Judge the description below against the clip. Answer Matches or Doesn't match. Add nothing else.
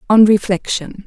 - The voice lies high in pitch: Matches